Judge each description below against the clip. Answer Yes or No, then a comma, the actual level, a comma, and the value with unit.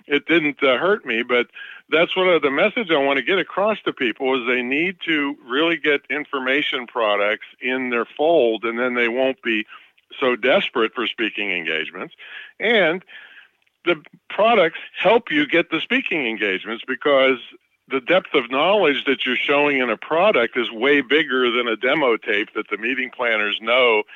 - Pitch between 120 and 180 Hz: Yes, medium, 140 Hz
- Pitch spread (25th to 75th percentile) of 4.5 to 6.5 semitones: Yes, average, 5.1 semitones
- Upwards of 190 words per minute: No, average, 175 wpm